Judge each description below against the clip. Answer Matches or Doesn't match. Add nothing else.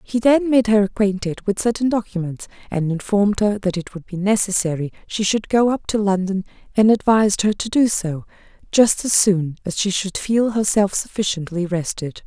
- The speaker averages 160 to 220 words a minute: Matches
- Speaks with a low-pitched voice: Doesn't match